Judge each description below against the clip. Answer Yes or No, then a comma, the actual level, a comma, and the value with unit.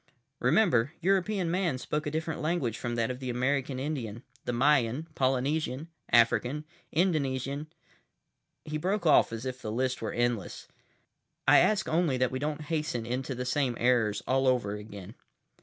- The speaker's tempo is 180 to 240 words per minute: No, average, 155 wpm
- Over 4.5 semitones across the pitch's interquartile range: No, average, 4.1 semitones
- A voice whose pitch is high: No, low, 130 Hz